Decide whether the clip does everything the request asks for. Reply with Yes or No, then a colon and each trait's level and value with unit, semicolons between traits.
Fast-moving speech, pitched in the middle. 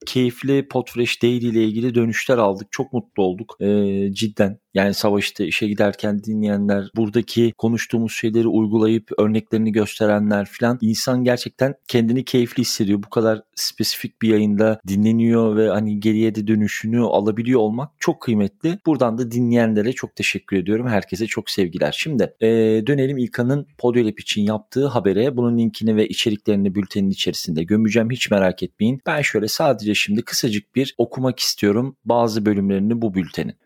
No: fast, 150 wpm; low, 110 Hz